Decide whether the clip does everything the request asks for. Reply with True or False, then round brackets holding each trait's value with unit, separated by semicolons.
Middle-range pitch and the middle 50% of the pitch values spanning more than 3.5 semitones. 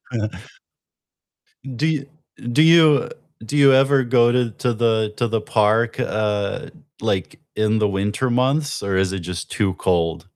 False (115 Hz; 4.1 semitones)